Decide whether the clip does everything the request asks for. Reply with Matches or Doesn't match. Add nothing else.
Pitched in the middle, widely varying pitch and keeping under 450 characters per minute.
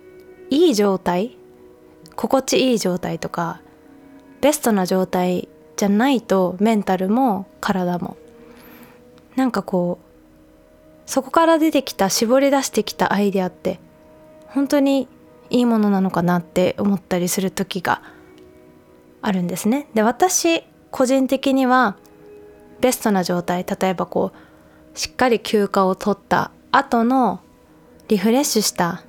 Doesn't match